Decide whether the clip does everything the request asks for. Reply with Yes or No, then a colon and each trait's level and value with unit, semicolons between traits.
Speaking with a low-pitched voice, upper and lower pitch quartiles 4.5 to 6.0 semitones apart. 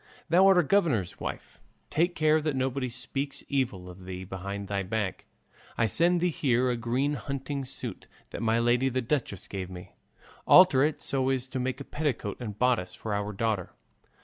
Yes: low, 125 Hz; wide, 5.6 semitones